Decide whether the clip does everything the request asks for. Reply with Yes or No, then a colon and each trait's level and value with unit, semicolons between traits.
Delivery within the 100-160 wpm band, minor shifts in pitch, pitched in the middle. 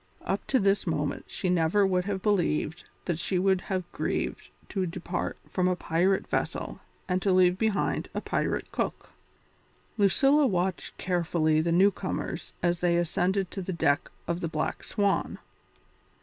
Yes: average, 155 wpm; narrow, 2.1 semitones; medium, 180 Hz